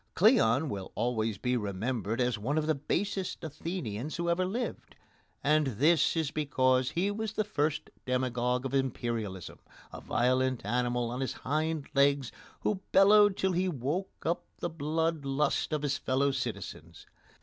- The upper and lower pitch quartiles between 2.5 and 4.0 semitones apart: No, average, 5.0 semitones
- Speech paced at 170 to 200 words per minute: No, average, 155 wpm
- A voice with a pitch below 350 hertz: Yes, medium, 140 Hz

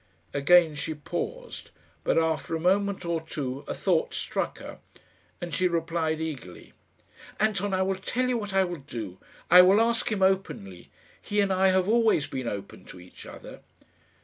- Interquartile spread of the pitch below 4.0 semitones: No, average, 4.6 semitones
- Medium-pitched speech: Yes, medium, 175 Hz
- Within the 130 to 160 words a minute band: No, average, 175 wpm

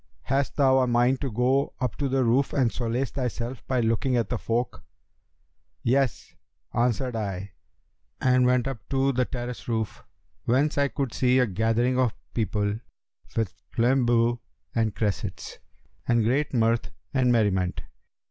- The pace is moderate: Yes, average, 150 wpm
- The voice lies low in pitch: Yes, low, 120 Hz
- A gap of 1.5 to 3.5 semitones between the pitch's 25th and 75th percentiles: Yes, narrow, 2.4 semitones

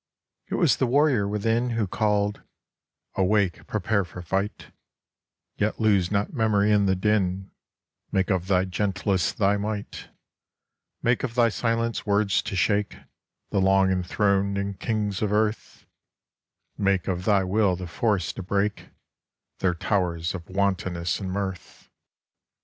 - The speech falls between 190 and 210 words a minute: No, average, 140 wpm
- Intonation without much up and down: Yes, narrow, 2.1 semitones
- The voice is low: Yes, low, 100 Hz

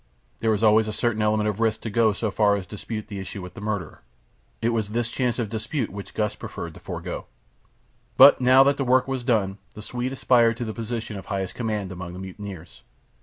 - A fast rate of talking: Yes, fast, 225 wpm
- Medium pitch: No, low, 110 Hz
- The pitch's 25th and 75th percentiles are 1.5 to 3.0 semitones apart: Yes, average, 2.7 semitones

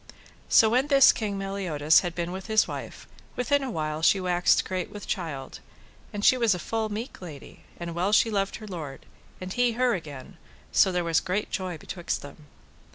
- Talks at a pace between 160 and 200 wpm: Yes, average, 195 wpm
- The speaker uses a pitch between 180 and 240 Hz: Yes, high, 190 Hz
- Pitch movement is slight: No, average, 4.4 semitones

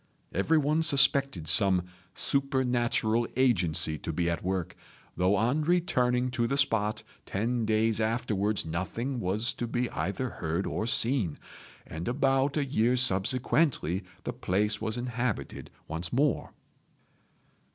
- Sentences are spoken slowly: Yes, slow, 125 wpm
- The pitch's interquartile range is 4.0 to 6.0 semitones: Yes, average, 5.2 semitones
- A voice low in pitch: Yes, low, 115 Hz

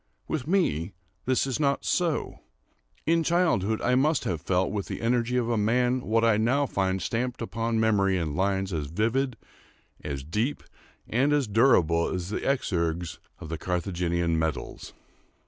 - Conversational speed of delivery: Yes, average, 160 wpm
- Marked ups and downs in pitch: Yes, wide, 6.1 semitones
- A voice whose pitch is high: No, low, 110 Hz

